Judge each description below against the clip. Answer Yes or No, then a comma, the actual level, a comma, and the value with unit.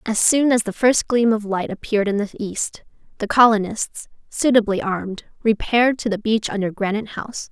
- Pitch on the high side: Yes, high, 215 Hz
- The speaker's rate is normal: Yes, average, 185 wpm